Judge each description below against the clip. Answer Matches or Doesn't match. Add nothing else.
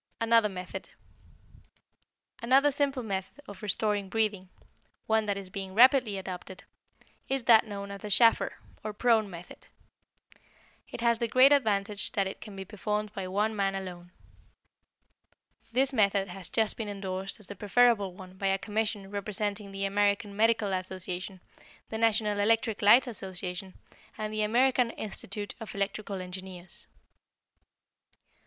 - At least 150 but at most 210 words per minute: Doesn't match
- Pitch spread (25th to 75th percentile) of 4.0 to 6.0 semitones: Doesn't match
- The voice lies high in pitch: Matches